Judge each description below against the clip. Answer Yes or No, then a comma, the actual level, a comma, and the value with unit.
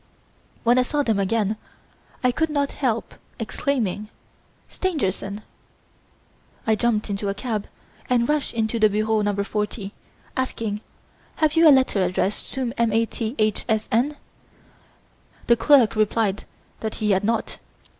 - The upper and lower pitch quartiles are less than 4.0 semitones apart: Yes, average, 3.2 semitones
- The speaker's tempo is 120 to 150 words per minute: Yes, average, 145 wpm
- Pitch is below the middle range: No, high, 220 Hz